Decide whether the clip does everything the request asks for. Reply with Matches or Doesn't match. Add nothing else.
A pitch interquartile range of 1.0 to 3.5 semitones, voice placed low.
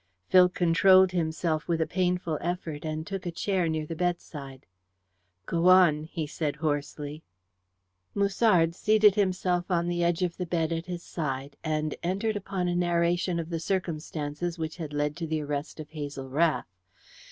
Doesn't match